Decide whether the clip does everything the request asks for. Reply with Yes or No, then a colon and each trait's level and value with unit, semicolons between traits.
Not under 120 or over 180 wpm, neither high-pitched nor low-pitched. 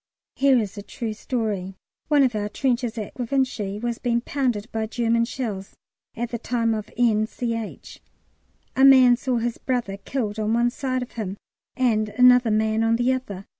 No: average, 175 wpm; high, 235 Hz